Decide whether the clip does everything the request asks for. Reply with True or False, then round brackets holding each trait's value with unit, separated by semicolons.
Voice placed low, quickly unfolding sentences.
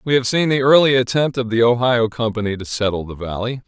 True (120 Hz; 230 wpm)